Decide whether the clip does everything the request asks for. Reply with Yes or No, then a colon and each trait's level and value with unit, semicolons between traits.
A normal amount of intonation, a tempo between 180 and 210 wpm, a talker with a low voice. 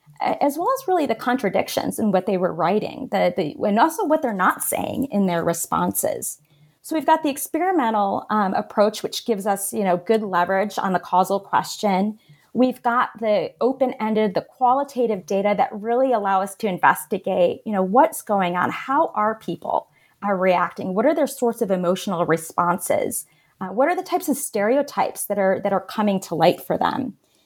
No: average, 4.9 semitones; average, 190 wpm; high, 210 Hz